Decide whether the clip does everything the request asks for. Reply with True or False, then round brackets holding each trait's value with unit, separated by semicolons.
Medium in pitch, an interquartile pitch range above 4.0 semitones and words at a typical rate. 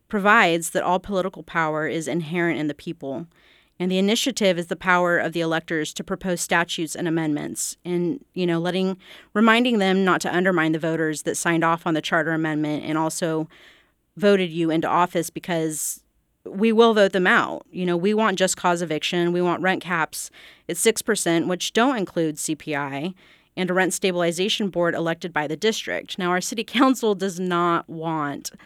False (175 Hz; 2.7 semitones; 180 wpm)